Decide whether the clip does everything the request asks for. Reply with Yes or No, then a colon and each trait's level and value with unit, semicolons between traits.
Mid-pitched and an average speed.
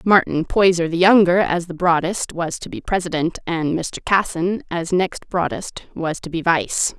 Yes: medium, 175 Hz; average, 180 wpm